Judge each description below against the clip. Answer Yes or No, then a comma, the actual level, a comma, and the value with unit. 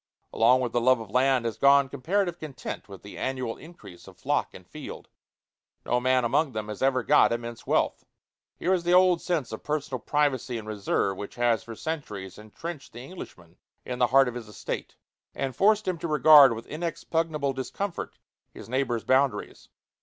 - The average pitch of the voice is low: Yes, low, 130 Hz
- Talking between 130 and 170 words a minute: No, average, 185 wpm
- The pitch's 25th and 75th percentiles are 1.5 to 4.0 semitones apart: No, average, 4.8 semitones